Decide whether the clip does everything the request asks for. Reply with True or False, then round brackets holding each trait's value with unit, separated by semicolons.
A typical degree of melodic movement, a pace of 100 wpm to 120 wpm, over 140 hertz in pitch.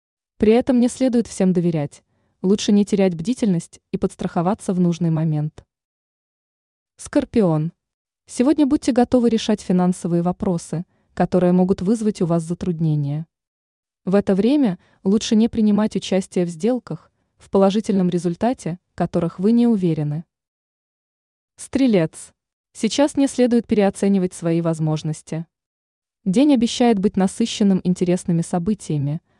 True (4.8 semitones; 115 wpm; 190 Hz)